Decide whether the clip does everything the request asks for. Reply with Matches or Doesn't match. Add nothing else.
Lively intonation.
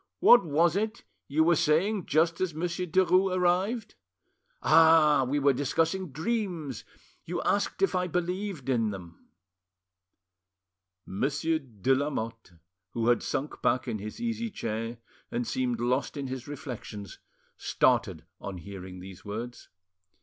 Matches